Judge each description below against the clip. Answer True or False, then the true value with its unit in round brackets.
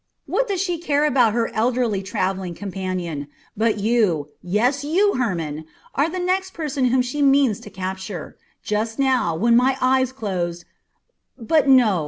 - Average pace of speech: True (155 wpm)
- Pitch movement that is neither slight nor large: False (6.4 semitones)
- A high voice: True (235 Hz)